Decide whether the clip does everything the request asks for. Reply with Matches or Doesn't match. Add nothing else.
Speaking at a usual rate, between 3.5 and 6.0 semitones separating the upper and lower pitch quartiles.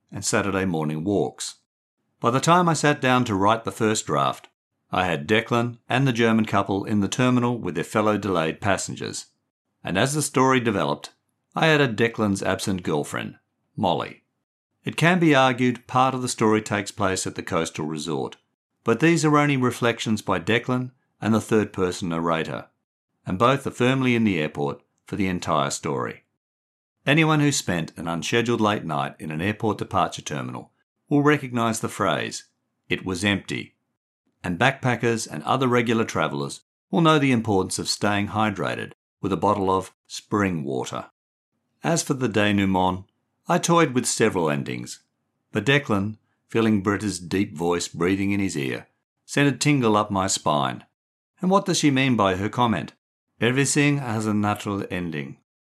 Matches